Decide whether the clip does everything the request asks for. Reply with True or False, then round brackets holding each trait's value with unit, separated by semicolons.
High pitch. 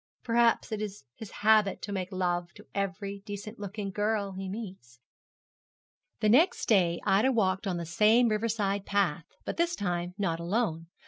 True (200 Hz)